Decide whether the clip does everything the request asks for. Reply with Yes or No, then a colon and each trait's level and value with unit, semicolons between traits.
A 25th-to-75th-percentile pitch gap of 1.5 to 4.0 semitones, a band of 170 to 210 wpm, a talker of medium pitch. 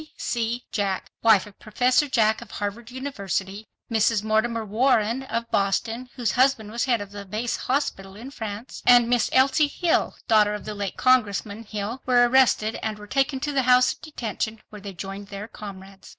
No: average, 3.4 semitones; average, 180 wpm; high, 225 Hz